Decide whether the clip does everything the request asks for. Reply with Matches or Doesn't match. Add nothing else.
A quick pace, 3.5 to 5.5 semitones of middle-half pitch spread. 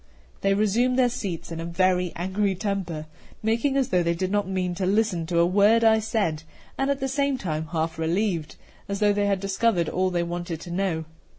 Matches